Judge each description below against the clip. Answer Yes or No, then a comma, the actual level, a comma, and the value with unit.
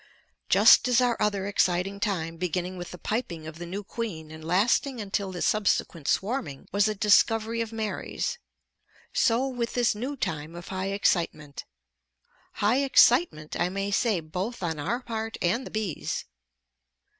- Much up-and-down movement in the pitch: No, average, 4.8 semitones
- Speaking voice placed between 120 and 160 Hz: No, high, 200 Hz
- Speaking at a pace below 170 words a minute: Yes, average, 155 wpm